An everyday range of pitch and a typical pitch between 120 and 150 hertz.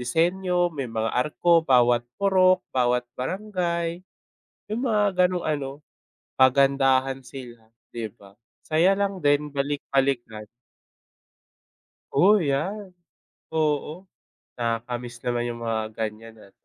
No: wide, 6.5 semitones; medium, 140 Hz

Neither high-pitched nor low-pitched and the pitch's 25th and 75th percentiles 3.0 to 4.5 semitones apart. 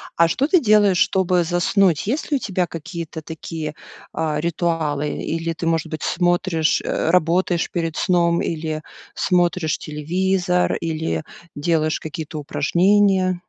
No: medium, 170 Hz; narrow, 2.5 semitones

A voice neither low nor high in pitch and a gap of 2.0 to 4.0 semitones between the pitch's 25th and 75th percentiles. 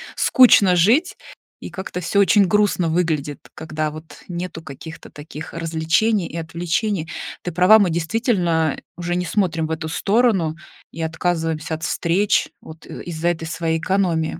Yes: medium, 170 Hz; average, 2.9 semitones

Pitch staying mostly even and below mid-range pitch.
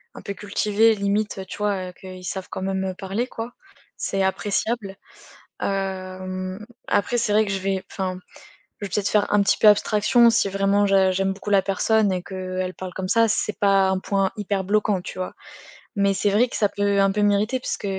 No: narrow, 1.6 semitones; high, 195 Hz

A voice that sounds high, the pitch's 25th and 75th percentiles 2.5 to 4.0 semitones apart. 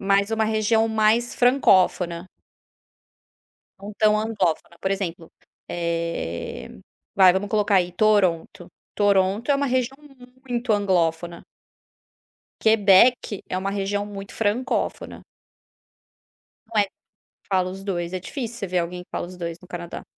Yes: high, 195 Hz; average, 3.4 semitones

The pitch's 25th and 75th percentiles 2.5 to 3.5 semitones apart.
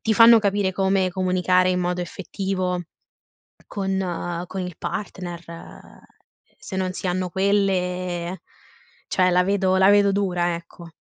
No: narrow, 1.4 semitones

